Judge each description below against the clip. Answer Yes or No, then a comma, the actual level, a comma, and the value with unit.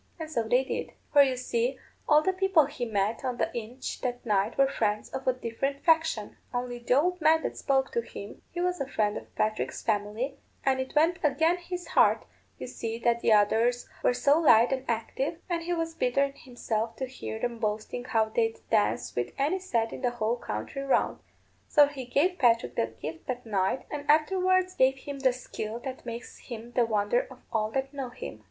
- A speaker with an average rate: No, fast, 210 wpm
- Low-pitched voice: No, very high, 255 Hz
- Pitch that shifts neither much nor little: Yes, average, 4.4 semitones